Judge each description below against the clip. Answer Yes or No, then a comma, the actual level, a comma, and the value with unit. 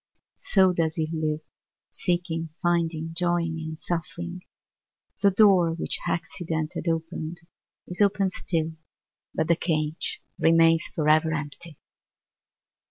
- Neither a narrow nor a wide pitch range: No, narrow, 1.6 semitones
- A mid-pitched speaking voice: Yes, medium, 165 Hz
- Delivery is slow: Yes, slow, 110 wpm